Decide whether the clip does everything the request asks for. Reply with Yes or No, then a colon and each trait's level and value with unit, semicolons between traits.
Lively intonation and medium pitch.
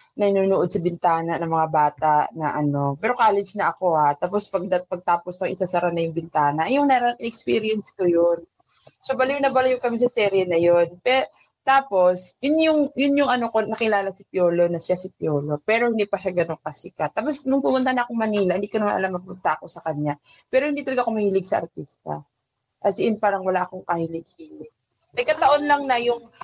No: wide, 6.0 semitones; high, 195 Hz